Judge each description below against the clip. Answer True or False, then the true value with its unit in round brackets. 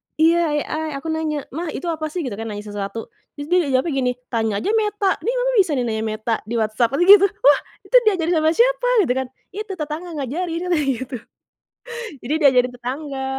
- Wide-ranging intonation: True (6.1 semitones)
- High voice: True (300 Hz)